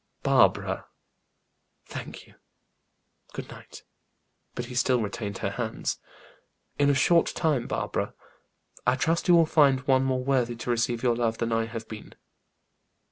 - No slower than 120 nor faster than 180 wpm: Yes, average, 145 wpm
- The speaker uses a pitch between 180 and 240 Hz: No, low, 125 Hz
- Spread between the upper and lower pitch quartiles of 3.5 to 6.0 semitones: No, average, 3.1 semitones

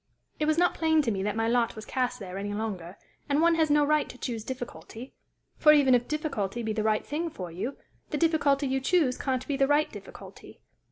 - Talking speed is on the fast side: Yes, fast, 225 wpm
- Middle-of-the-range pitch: No, very high, 260 Hz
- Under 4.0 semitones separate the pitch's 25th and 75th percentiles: No, wide, 5.5 semitones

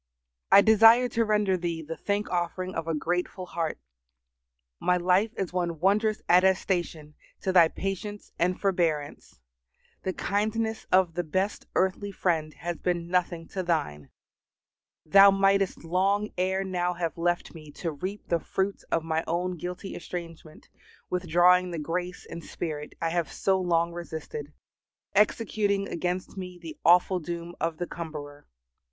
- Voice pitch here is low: No, medium, 180 Hz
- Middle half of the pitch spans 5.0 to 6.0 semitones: No, narrow, 2.6 semitones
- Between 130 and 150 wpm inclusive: Yes, average, 145 wpm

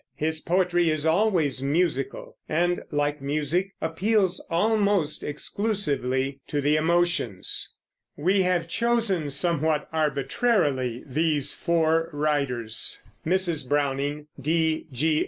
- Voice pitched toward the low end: No, medium, 155 Hz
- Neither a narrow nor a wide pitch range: Yes, average, 3.6 semitones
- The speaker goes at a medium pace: No, slow, 100 wpm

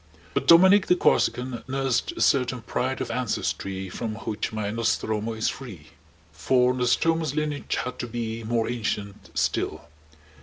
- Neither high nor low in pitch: No, low, 120 Hz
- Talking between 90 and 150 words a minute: Yes, average, 145 wpm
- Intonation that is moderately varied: Yes, average, 3.2 semitones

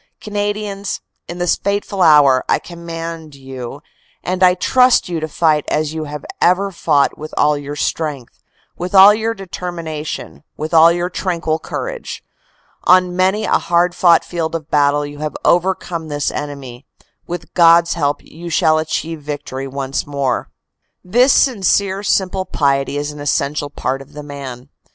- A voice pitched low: No, medium, 165 Hz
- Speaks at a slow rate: No, average, 160 wpm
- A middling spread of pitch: Yes, average, 3.9 semitones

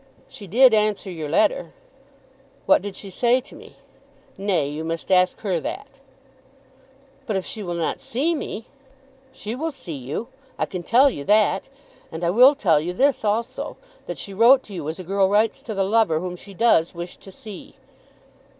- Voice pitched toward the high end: Yes, high, 200 Hz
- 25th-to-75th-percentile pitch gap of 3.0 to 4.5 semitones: No, average, 4.9 semitones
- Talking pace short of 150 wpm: No, average, 185 wpm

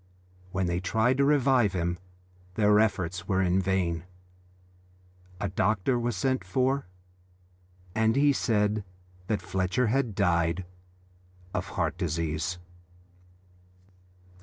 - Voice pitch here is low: Yes, low, 100 Hz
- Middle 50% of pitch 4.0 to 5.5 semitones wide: Yes, average, 5.0 semitones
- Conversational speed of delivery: No, slow, 110 wpm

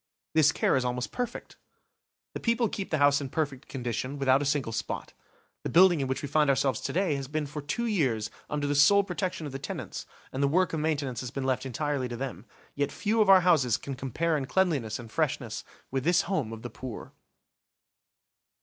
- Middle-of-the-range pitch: Yes, medium, 145 Hz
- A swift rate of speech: Yes, fast, 215 wpm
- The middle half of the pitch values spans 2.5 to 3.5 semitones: No, average, 4.2 semitones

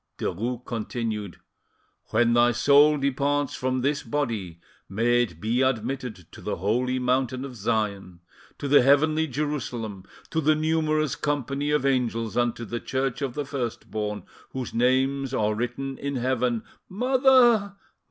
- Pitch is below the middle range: Yes, low, 130 Hz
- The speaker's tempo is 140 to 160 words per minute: Yes, average, 145 wpm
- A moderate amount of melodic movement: Yes, average, 3.6 semitones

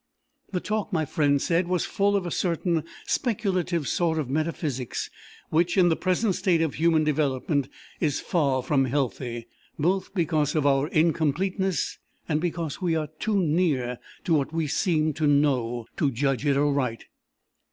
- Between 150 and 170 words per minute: Yes, average, 160 wpm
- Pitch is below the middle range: No, medium, 155 Hz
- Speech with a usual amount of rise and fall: Yes, average, 3.8 semitones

